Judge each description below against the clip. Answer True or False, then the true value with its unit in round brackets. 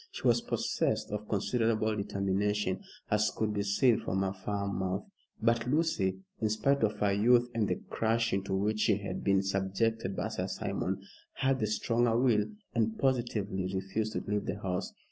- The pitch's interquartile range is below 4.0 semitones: True (2.7 semitones)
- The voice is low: True (105 Hz)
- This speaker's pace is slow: False (175 wpm)